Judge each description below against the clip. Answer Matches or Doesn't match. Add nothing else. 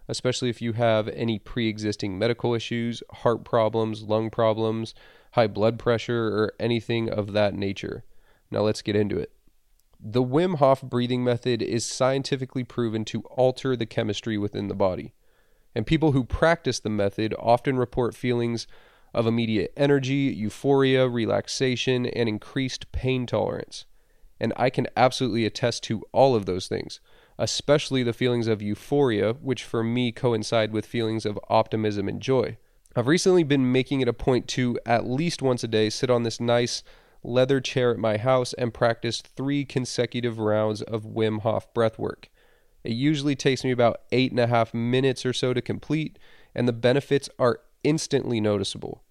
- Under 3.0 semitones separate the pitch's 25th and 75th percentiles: Matches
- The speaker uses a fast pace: Doesn't match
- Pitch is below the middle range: Matches